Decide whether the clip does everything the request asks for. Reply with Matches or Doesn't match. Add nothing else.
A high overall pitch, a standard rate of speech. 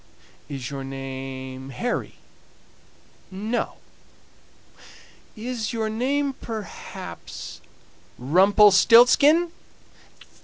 Doesn't match